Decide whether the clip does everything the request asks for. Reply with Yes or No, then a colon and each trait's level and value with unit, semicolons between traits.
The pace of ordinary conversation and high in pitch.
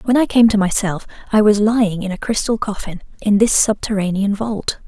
Yes: average, 195 wpm; high, 210 Hz